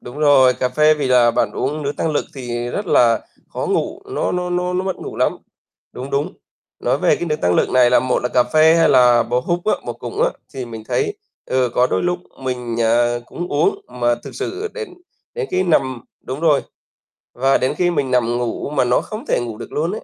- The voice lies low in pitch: Yes, low, 130 Hz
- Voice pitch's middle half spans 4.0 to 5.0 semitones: No, wide, 5.5 semitones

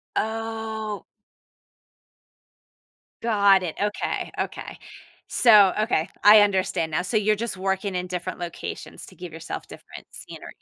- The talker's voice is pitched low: No, high, 200 Hz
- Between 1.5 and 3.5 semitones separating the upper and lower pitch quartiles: Yes, average, 3.0 semitones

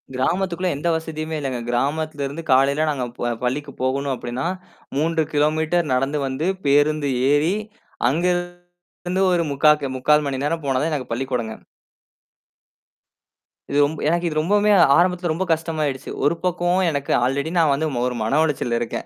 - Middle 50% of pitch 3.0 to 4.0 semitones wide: Yes, average, 3.6 semitones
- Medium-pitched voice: Yes, medium, 150 Hz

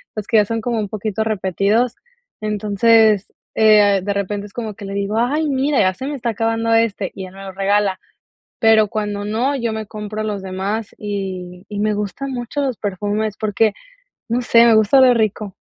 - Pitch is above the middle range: Yes, high, 215 Hz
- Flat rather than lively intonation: Yes, narrow, 2.2 semitones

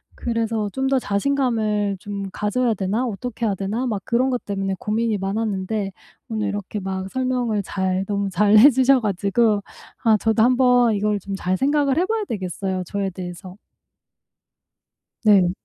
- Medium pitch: No, high, 210 Hz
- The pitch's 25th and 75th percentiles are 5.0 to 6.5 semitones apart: No, average, 3.7 semitones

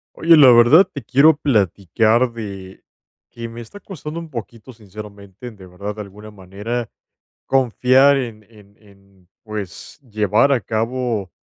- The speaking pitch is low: Yes, low, 110 Hz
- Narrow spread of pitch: No, average, 4.0 semitones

